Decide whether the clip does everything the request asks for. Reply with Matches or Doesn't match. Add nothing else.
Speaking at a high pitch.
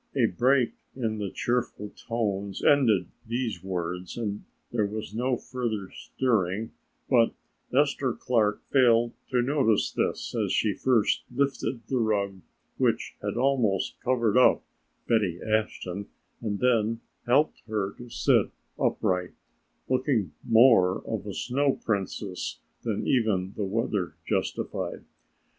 Doesn't match